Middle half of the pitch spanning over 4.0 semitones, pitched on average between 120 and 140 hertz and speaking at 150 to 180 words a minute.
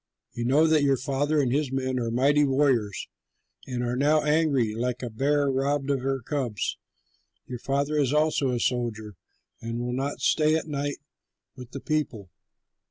No: average, 2.9 semitones; low, 135 Hz; average, 170 wpm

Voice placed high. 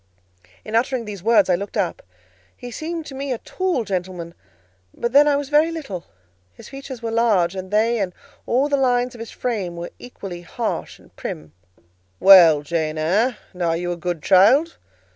Yes: high, 215 Hz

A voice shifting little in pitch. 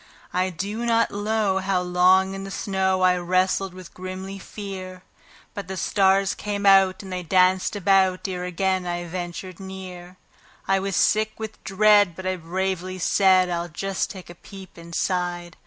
Yes: narrow, 1.3 semitones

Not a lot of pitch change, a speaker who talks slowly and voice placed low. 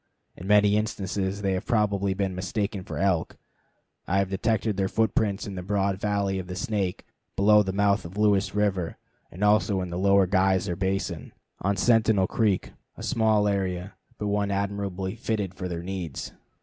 No: narrow, 1.7 semitones; average, 175 wpm; low, 100 Hz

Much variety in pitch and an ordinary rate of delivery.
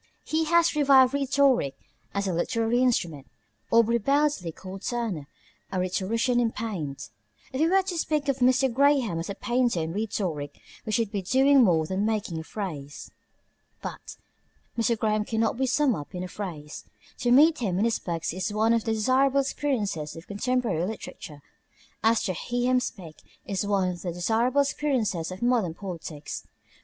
Yes: wide, 6.0 semitones; average, 170 wpm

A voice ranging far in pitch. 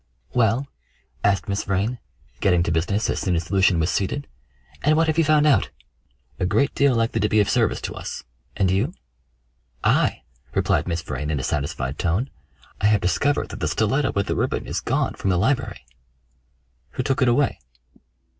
Yes: wide, 6.8 semitones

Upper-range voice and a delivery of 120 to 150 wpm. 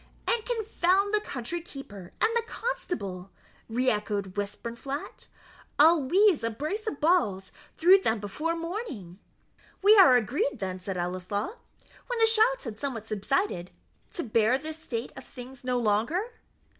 Yes: very high, 265 Hz; average, 145 wpm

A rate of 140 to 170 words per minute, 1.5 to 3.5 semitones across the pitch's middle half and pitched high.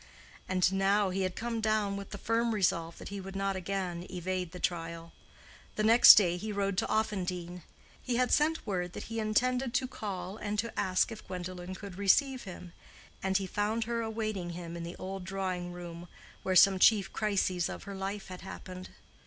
No: average, 195 wpm; average, 3.1 semitones; high, 195 Hz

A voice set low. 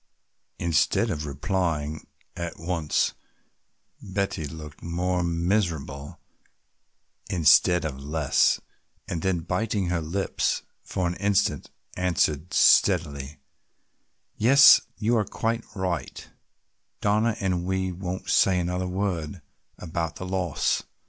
Yes: very low, 90 Hz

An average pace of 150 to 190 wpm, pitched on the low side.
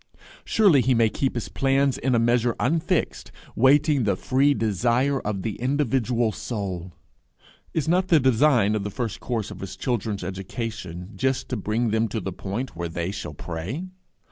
Yes: average, 170 wpm; low, 115 Hz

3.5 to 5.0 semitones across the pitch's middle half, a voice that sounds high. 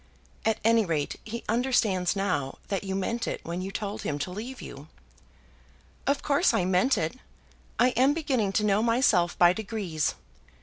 Yes: average, 4.7 semitones; high, 205 Hz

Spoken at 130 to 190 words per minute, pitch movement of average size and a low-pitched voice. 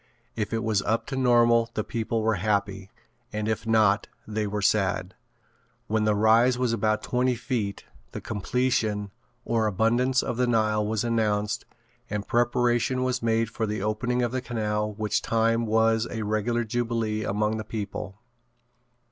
No: average, 160 wpm; narrow, 1.8 semitones; low, 110 Hz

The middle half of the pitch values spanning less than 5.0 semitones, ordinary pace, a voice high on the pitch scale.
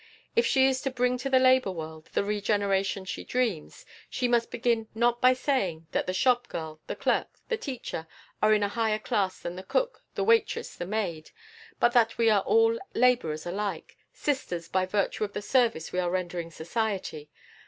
No: wide, 5.5 semitones; average, 190 wpm; high, 215 Hz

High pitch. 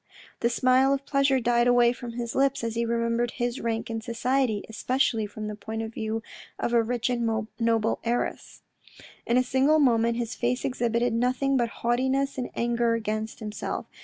Yes: high, 235 Hz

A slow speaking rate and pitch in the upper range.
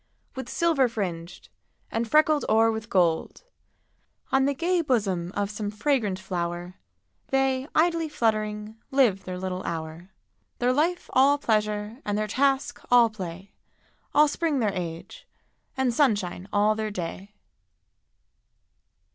Yes: slow, 130 wpm; high, 215 Hz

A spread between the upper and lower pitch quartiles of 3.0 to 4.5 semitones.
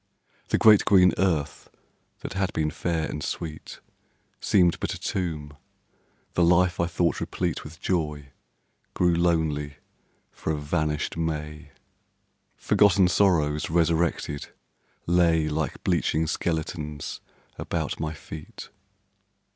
No: narrow, 2.5 semitones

